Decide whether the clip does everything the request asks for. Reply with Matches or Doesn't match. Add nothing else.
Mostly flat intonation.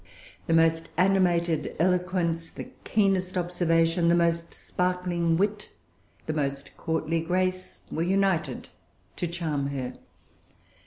Matches